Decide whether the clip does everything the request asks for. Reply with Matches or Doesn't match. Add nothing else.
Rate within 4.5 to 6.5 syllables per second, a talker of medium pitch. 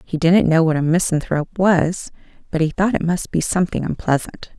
Matches